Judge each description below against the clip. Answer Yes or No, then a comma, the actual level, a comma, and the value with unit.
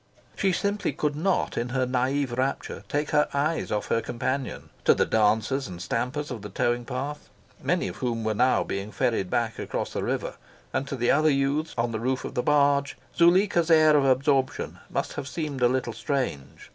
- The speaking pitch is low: Yes, low, 130 Hz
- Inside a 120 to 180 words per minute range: No, average, 195 wpm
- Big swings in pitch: No, average, 3.8 semitones